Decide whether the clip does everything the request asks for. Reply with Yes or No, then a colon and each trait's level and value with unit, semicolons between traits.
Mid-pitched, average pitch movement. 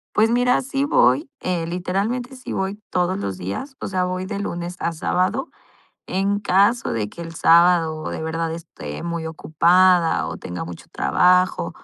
Yes: medium, 180 Hz; average, 3.4 semitones